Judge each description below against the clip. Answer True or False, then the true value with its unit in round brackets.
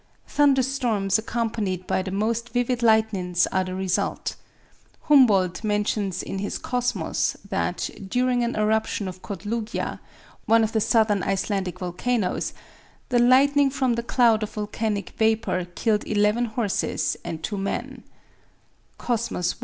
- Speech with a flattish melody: False (3.5 semitones)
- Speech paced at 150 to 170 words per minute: False (135 wpm)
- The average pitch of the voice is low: False (220 Hz)